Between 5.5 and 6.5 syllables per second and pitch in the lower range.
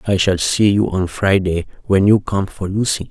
No: 4.7 syllables/s; very low, 95 Hz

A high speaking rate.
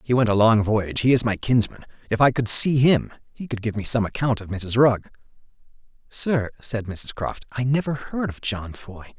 Yes: fast, 215 wpm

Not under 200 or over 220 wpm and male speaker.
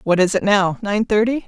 No: fast, 205 wpm; female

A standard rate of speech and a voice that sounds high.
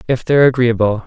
No: average, 170 wpm; low, 120 Hz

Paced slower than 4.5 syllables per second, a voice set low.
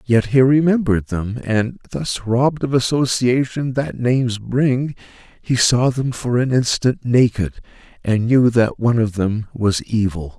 Yes: 4.3 syllables/s; low, 120 Hz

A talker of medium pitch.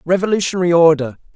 Yes: medium, 170 Hz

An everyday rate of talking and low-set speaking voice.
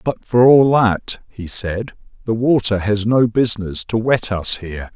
Yes: average, 180 wpm; low, 110 Hz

